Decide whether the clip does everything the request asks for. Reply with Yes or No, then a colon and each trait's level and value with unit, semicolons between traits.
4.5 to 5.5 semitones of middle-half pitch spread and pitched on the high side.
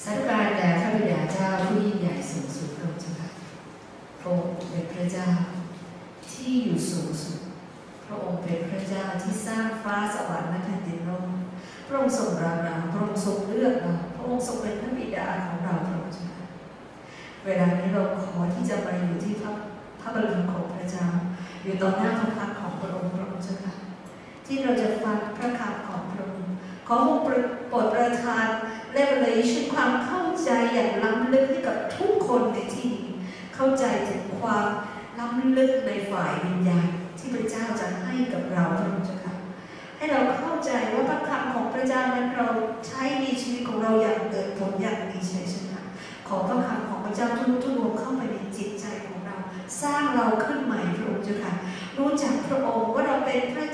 Yes: average, 4.8 semitones; high, 210 Hz